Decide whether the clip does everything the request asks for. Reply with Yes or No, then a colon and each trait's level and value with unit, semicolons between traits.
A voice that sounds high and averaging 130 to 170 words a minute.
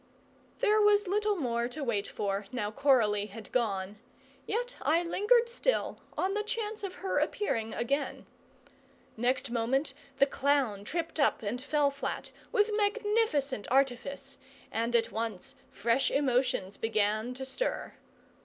Yes: very high, 270 Hz; slow, 135 wpm